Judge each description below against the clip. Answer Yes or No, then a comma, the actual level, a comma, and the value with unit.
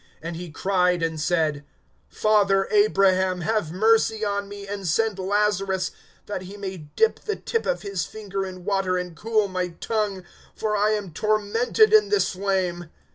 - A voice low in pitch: No, high, 195 Hz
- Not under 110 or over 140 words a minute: No, average, 165 wpm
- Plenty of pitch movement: No, average, 2.7 semitones